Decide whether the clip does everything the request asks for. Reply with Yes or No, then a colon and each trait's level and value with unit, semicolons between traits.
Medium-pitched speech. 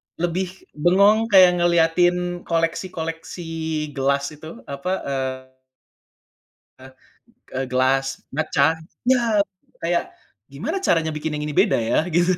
Yes: medium, 165 Hz